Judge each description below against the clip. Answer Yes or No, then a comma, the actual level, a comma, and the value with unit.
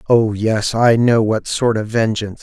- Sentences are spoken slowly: No, average, 200 wpm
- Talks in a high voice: No, low, 110 Hz